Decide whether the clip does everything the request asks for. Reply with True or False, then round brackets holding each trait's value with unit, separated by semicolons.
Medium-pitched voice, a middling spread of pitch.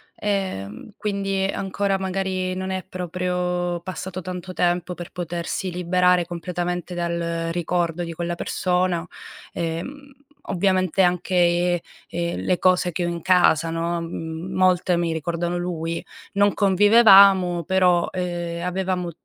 False (180 Hz; 1.5 semitones)